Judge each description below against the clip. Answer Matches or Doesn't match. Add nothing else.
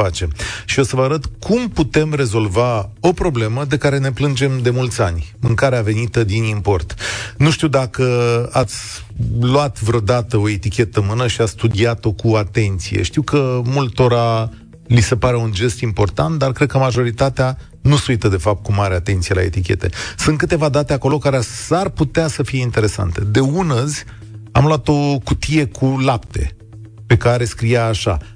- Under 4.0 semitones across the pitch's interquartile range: Doesn't match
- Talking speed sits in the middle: Doesn't match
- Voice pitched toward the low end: Matches